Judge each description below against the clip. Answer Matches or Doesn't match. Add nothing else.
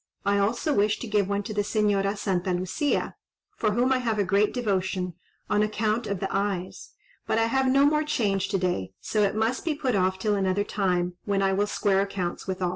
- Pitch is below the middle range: Doesn't match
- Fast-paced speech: Matches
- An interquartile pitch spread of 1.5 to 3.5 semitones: Matches